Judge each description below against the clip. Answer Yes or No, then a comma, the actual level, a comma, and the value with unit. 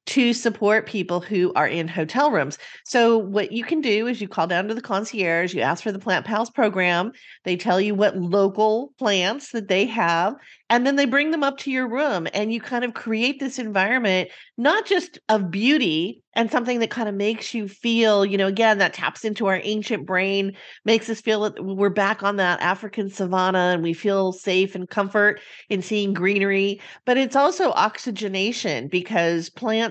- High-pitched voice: Yes, high, 210 Hz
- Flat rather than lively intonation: No, average, 3.5 semitones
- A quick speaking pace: No, average, 195 wpm